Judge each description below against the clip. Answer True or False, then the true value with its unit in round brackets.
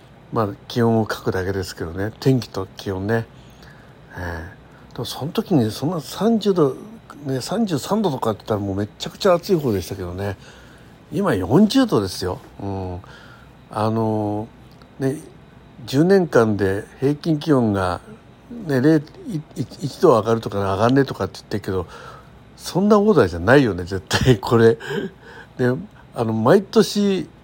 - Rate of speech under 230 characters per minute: False (260 characters per minute)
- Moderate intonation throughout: False (7.0 semitones)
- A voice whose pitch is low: True (125 Hz)